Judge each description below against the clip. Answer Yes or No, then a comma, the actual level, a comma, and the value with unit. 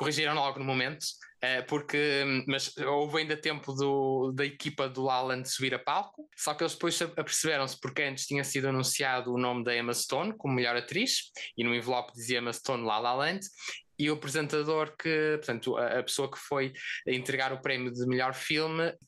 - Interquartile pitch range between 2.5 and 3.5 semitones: Yes, average, 2.9 semitones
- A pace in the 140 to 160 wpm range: No, fast, 185 wpm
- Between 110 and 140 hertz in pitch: Yes, low, 135 Hz